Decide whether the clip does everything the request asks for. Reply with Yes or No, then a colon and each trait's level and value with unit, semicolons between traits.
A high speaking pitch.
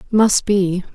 Yes: high, 195 Hz